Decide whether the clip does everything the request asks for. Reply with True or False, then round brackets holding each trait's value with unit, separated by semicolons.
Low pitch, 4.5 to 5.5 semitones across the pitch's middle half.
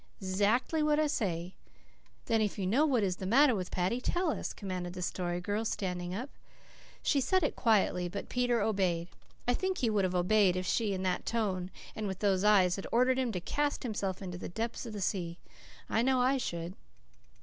False (205 Hz; 5.1 semitones)